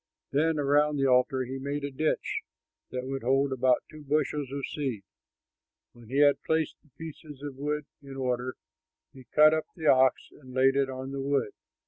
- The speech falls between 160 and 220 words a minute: Yes, average, 185 wpm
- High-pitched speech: No, medium, 140 Hz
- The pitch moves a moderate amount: No, narrow, 2.1 semitones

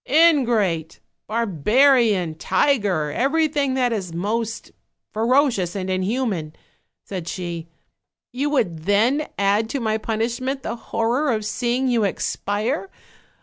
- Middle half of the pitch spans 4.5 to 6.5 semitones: Yes, wide, 5.4 semitones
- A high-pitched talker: Yes, high, 225 Hz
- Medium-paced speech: No, slow, 115 wpm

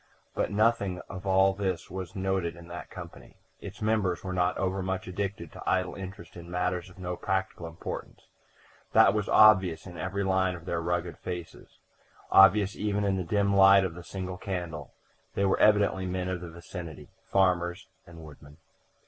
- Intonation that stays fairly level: Yes, narrow, 1.9 semitones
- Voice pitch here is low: Yes, very low, 95 Hz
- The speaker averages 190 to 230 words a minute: No, average, 175 wpm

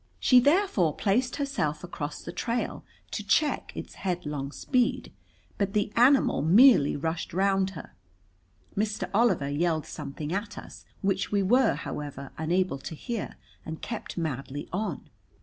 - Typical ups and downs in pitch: No, wide, 7.0 semitones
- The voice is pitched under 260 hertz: Yes, high, 190 Hz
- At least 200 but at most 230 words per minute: No, average, 140 wpm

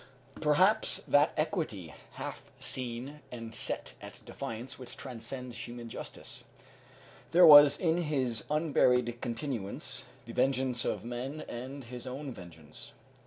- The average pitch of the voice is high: No, low, 125 Hz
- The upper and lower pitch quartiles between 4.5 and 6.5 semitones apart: No, average, 3.8 semitones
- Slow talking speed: Yes, slow, 120 wpm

